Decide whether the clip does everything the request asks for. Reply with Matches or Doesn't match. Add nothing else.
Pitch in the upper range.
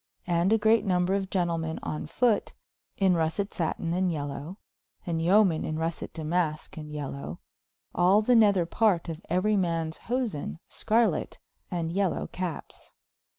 Doesn't match